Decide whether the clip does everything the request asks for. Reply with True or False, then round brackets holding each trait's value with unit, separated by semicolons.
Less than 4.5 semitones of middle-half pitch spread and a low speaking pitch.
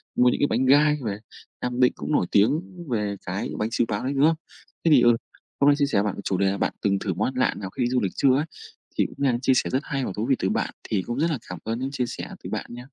False (4.8 semitones; 125 Hz)